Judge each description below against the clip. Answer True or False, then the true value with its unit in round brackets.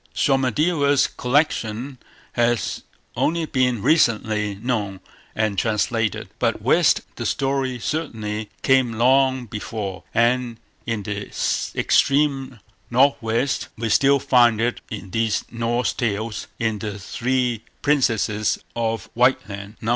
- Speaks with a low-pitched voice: True (120 Hz)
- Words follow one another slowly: True (115 wpm)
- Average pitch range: True (3.5 semitones)